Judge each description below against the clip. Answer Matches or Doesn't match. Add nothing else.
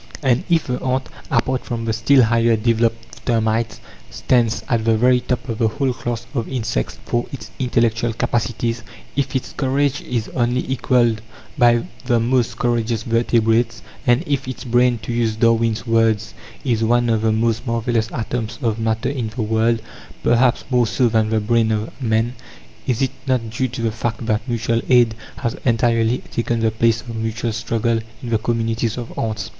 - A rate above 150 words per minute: Matches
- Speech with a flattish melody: Matches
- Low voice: Matches